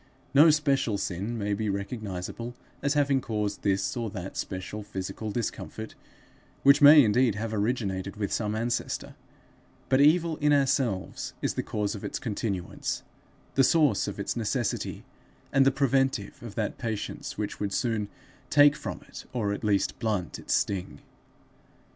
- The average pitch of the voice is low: Yes, low, 110 Hz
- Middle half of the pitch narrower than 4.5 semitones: No, average, 4.9 semitones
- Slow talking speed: No, average, 155 wpm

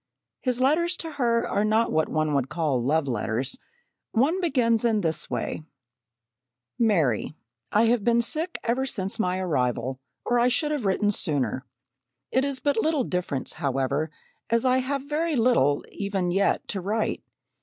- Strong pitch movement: Yes, wide, 8.6 semitones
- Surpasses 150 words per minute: Yes, average, 160 wpm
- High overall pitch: Yes, high, 215 Hz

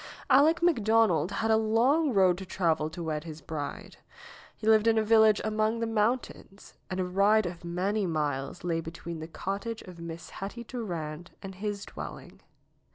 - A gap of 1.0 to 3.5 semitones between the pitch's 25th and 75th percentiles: No, average, 4.7 semitones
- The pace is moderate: Yes, average, 170 wpm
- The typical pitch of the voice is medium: No, high, 195 Hz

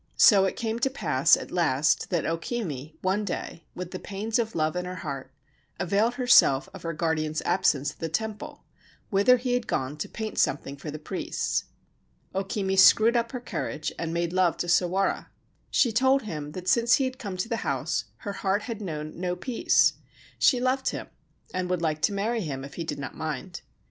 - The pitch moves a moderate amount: No, wide, 6.0 semitones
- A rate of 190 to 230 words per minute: Yes, fast, 205 wpm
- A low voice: No, medium, 185 Hz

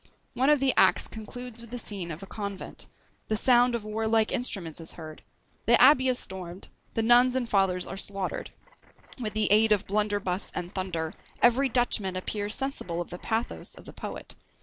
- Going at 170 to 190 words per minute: Yes, average, 185 wpm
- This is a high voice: Yes, high, 215 Hz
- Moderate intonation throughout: Yes, average, 4.3 semitones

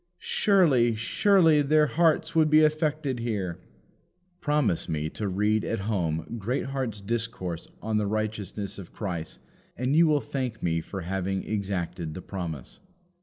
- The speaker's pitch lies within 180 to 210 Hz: No, low, 110 Hz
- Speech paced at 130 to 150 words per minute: Yes, average, 140 wpm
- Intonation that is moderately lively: No, wide, 7.7 semitones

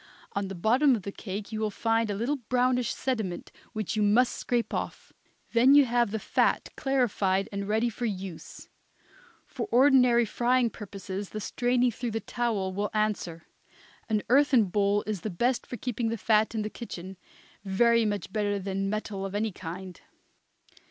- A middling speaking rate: Yes, average, 170 wpm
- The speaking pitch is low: No, high, 215 Hz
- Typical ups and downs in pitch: Yes, average, 3.4 semitones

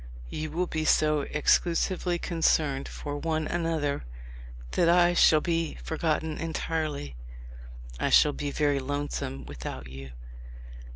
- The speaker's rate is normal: No, slow, 120 wpm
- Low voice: No, medium, 155 Hz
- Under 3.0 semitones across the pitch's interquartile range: Yes, narrow, 2.5 semitones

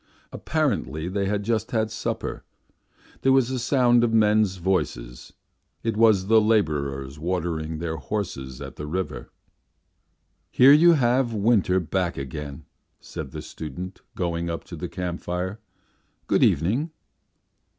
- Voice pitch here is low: Yes, very low, 95 Hz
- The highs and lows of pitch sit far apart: Yes, wide, 5.9 semitones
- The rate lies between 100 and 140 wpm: Yes, slow, 135 wpm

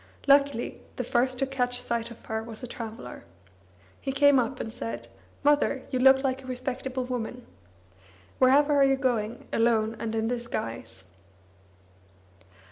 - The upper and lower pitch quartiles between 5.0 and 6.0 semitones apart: No, average, 2.8 semitones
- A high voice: Yes, very high, 250 Hz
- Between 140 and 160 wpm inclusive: Yes, average, 145 wpm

